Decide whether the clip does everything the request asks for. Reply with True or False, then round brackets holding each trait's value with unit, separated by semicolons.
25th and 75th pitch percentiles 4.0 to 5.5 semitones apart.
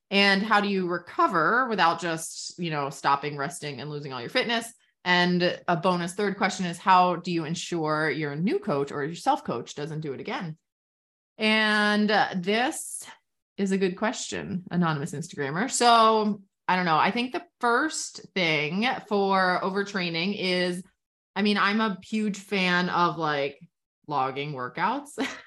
True (4.5 semitones)